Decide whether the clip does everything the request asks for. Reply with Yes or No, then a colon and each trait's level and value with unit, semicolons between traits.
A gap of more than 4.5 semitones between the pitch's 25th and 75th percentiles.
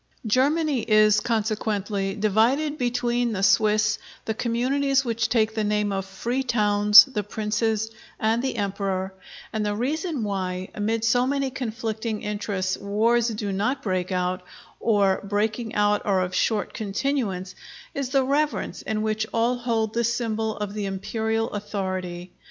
No: average, 2.8 semitones